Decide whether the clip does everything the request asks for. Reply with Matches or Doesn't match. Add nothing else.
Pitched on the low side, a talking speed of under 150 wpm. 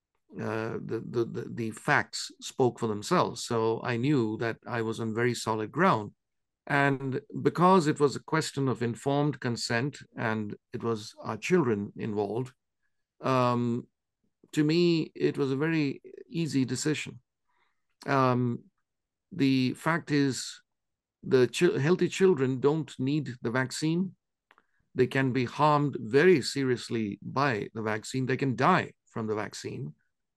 Matches